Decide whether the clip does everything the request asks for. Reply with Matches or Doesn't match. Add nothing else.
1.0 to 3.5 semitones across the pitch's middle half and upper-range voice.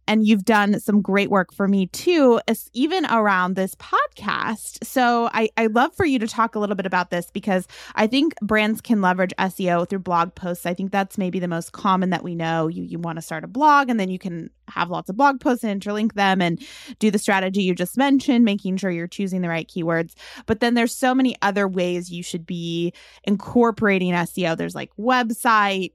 Doesn't match